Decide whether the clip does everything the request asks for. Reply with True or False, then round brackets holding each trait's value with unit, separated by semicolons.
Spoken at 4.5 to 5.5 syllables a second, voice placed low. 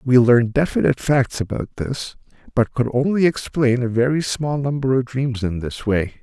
True (5.0 syllables/s; 125 Hz)